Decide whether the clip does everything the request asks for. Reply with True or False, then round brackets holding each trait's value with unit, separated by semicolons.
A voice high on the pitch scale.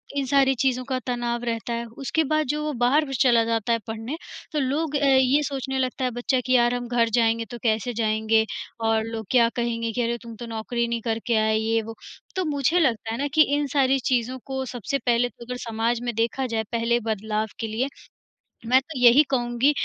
True (240 Hz)